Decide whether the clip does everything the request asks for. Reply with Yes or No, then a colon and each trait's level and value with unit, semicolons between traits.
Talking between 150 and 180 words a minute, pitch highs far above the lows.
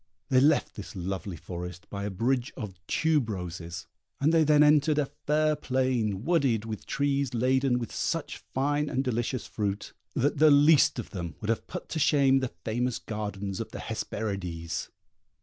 Yes: average, 170 wpm; wide, 6.0 semitones